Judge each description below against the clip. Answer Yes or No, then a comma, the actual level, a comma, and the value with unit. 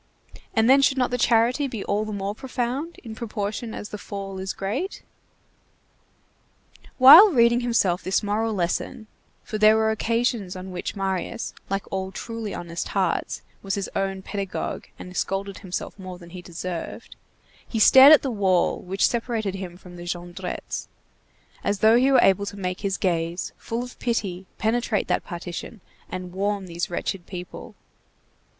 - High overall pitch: Yes, high, 200 Hz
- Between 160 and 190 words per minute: Yes, average, 165 wpm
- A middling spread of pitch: Yes, average, 3.8 semitones